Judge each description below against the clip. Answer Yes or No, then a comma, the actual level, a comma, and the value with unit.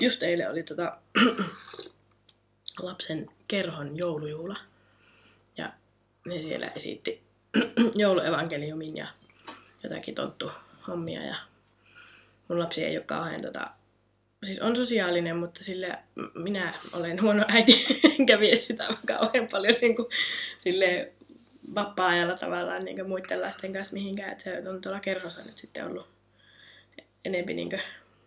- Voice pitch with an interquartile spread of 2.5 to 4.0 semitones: No, average, 5.0 semitones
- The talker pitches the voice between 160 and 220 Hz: Yes, medium, 185 Hz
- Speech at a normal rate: Yes, average, 125 wpm